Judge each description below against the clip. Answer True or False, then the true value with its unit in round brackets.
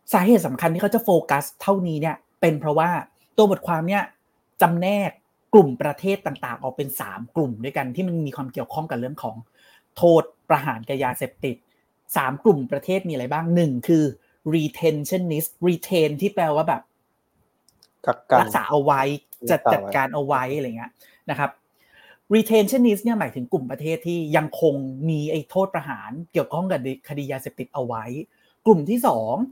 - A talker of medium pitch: True (160 Hz)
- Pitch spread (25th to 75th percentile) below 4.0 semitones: False (4.9 semitones)